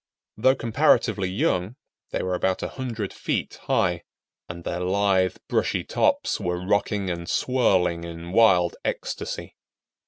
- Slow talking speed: Yes, slow, 125 wpm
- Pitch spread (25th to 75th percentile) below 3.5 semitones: Yes, average, 2.8 semitones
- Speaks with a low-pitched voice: Yes, very low, 95 Hz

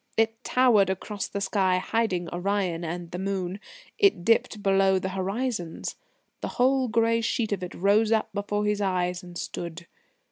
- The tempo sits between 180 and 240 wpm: No, average, 165 wpm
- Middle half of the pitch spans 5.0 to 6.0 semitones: No, average, 3.6 semitones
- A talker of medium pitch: No, high, 195 Hz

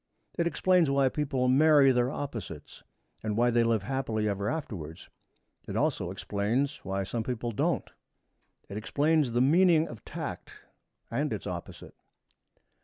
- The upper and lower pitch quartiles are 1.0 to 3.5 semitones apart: No, average, 5.0 semitones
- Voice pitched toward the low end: Yes, low, 125 Hz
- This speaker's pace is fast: No, average, 140 wpm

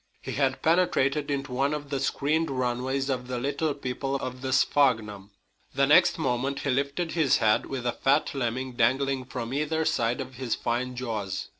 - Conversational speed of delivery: Yes, average, 180 wpm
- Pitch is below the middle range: Yes, low, 130 Hz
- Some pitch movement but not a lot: No, narrow, 2.2 semitones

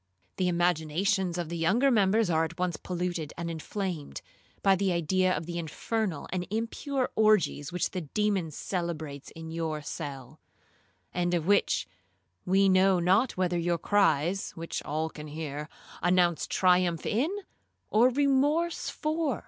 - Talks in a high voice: No, medium, 180 Hz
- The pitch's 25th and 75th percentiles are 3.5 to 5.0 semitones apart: Yes, average, 3.9 semitones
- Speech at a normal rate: Yes, average, 145 wpm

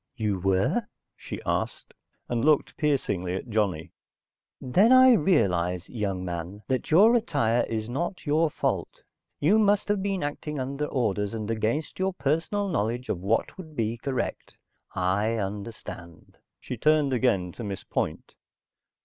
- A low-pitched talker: Yes, low, 120 Hz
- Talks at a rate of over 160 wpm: No, average, 145 wpm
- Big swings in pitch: Yes, wide, 7.5 semitones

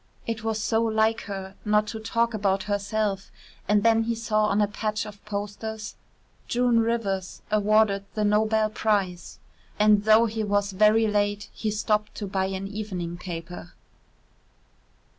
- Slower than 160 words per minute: Yes, average, 150 wpm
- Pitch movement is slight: Yes, narrow, 1.6 semitones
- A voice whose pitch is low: No, high, 210 Hz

